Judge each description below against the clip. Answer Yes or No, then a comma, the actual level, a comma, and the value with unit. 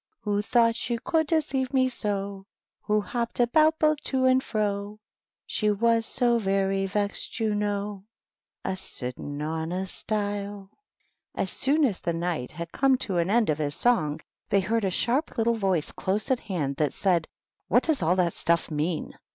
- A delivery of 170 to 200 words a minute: Yes, average, 180 wpm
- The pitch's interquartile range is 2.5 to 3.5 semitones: No, average, 4.7 semitones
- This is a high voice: Yes, high, 205 Hz